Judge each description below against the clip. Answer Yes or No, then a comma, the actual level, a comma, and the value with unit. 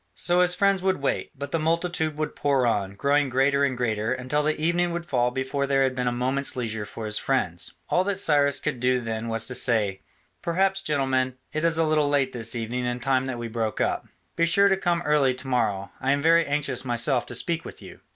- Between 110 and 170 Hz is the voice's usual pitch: Yes, low, 135 Hz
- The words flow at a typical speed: No, fast, 230 wpm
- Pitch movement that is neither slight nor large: Yes, average, 4.3 semitones